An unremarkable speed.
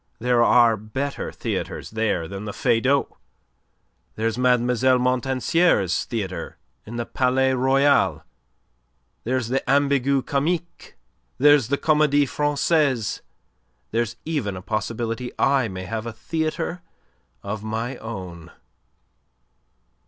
No: slow, 110 wpm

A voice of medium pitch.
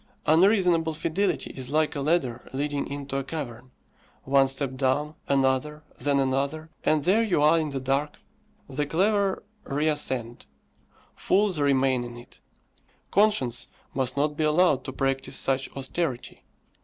Yes: medium, 145 Hz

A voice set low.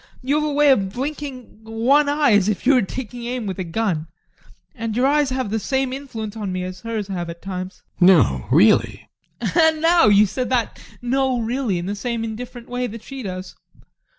No: high, 230 Hz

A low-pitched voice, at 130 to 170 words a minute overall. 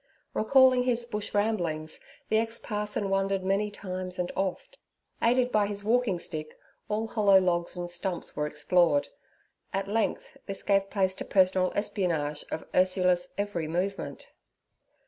No: high, 195 Hz; average, 145 wpm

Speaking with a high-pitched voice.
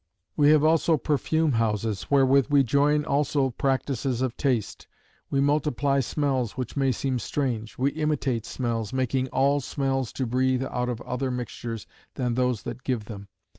No: low, 130 Hz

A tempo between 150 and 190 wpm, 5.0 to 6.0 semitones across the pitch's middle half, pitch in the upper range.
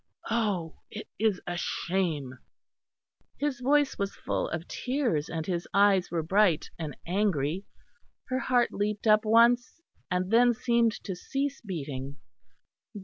No: slow, 135 wpm; wide, 5.6 semitones; high, 200 Hz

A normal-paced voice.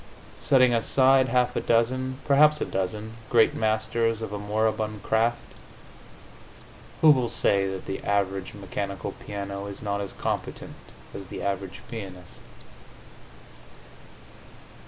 No: slow, 120 wpm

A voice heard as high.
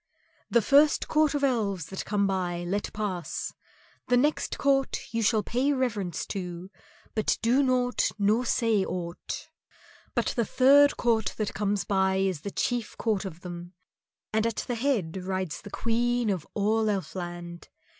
Yes: high, 210 Hz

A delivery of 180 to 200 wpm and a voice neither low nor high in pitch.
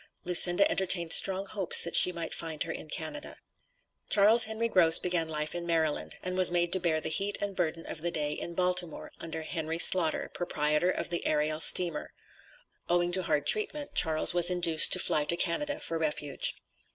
Yes: average, 190 wpm; medium, 170 Hz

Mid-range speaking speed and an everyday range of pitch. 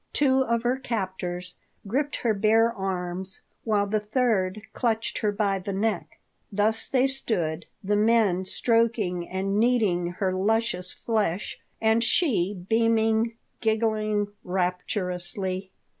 No: slow, 125 wpm; average, 3.3 semitones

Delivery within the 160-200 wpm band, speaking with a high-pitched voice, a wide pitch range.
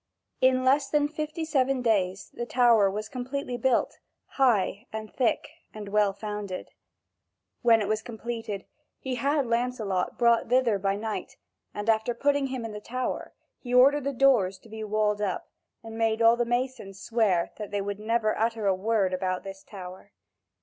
No: average, 170 wpm; high, 225 Hz; average, 3.6 semitones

